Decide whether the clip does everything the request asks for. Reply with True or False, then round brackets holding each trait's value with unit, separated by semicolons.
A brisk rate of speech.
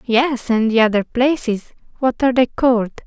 False (175 wpm)